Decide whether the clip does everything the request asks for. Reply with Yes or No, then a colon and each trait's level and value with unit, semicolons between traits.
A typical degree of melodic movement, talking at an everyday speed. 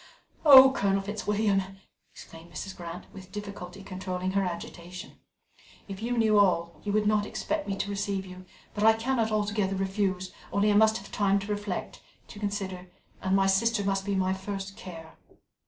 No: narrow, 1.8 semitones; average, 170 wpm